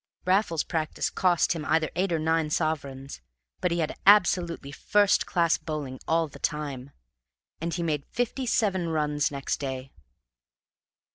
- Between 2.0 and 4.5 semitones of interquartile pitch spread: Yes, average, 3.1 semitones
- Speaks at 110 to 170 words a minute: Yes, average, 145 wpm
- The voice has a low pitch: No, medium, 160 Hz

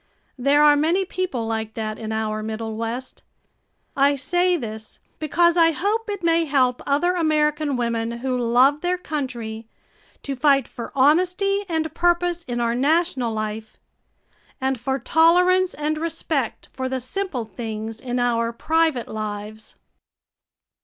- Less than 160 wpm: Yes, average, 140 wpm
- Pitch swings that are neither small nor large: No, wide, 6.2 semitones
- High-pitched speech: Yes, very high, 270 Hz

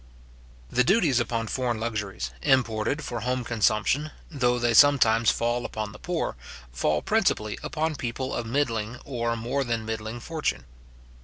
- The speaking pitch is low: Yes, low, 120 Hz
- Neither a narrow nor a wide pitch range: Yes, average, 3.0 semitones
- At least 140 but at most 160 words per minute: Yes, average, 145 wpm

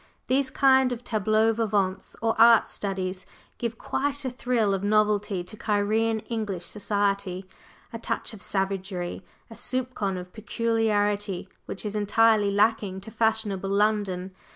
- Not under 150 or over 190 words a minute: No, slow, 135 wpm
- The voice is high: Yes, high, 210 Hz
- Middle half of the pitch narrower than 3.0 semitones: Yes, narrow, 2.5 semitones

